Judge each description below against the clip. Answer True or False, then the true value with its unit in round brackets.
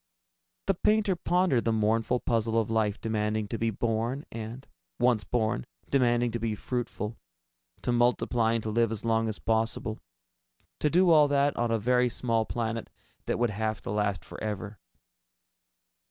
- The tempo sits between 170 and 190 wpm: False (160 wpm)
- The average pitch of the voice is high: False (115 Hz)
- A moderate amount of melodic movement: False (2.0 semitones)